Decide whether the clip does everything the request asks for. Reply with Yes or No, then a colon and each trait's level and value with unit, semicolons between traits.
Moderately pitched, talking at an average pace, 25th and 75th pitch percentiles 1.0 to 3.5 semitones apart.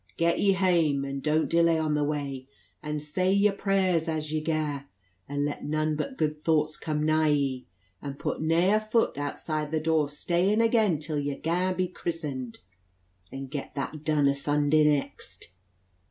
Yes: medium, 155 Hz; average, 175 wpm; narrow, 2.6 semitones